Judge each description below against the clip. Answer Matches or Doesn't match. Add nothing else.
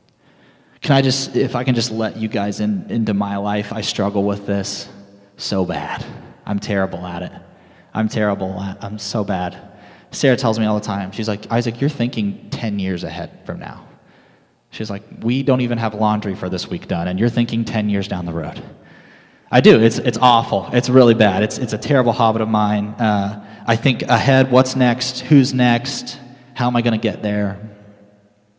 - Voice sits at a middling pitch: Doesn't match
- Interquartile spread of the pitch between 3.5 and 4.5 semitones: Doesn't match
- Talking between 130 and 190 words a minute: Doesn't match